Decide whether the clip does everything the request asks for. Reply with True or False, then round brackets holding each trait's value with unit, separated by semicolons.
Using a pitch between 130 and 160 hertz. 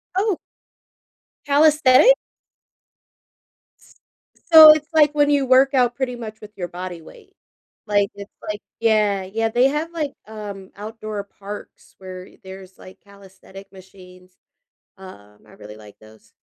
False (210 Hz)